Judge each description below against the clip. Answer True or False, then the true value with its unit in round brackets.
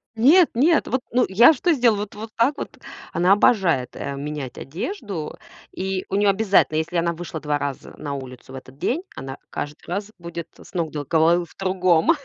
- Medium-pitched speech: True (175 Hz)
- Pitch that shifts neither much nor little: False (6.4 semitones)